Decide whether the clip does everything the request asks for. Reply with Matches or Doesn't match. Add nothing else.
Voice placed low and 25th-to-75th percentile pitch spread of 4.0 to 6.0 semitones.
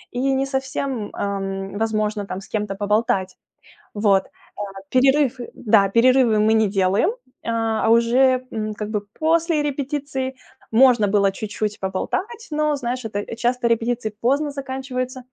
Doesn't match